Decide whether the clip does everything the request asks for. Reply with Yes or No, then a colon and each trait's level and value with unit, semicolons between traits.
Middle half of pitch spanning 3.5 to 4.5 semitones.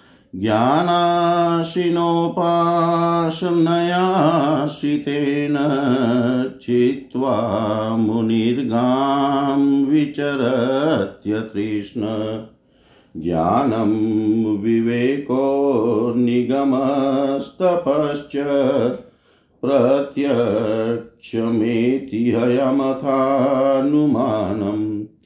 Yes: average, 4.1 semitones